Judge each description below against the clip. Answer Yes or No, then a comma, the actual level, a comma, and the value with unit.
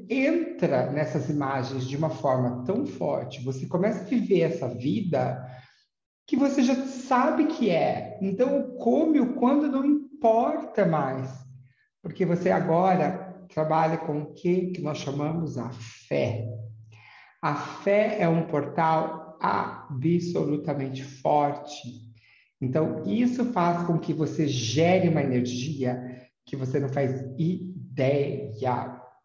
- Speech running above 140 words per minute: No, average, 125 wpm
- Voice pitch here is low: No, medium, 155 Hz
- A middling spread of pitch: No, wide, 6.5 semitones